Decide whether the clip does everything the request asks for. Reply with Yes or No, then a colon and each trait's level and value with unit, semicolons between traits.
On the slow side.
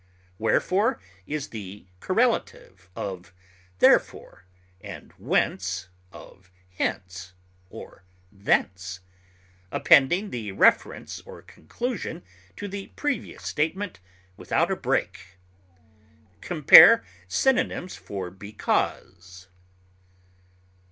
Yes: slow, 80 wpm